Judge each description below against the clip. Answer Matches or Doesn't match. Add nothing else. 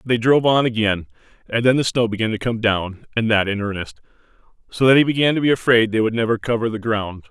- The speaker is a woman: Doesn't match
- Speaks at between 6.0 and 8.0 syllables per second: Matches